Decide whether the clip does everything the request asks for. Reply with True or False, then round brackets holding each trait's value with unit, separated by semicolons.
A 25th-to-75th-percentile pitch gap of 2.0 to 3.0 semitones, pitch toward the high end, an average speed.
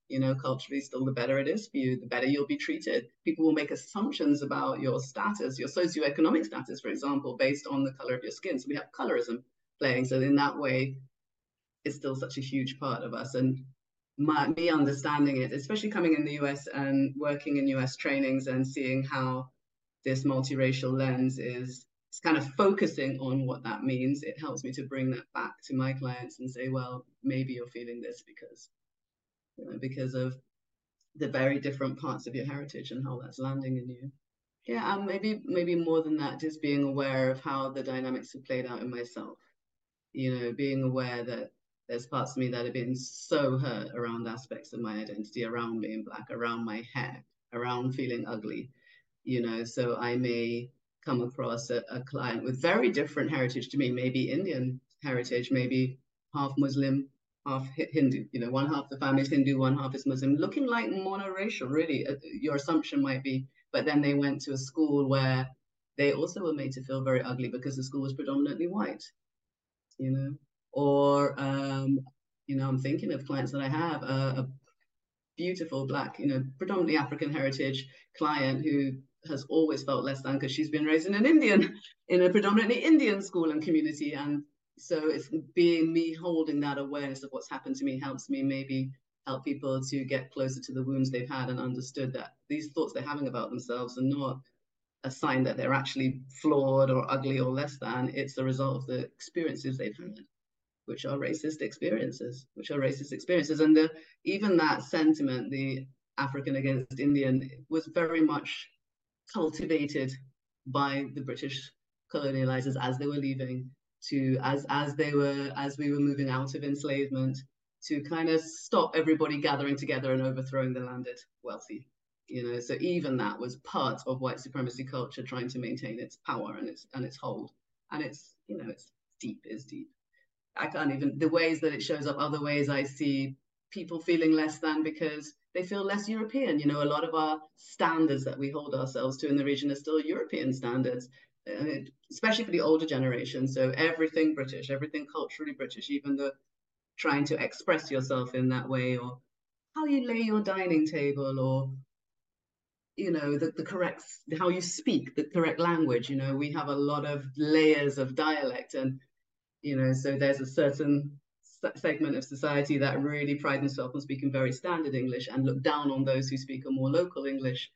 False (2.7 semitones; 135 Hz; 190 wpm)